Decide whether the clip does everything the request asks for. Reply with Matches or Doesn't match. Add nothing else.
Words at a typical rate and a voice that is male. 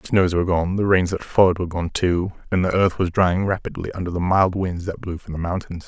Doesn't match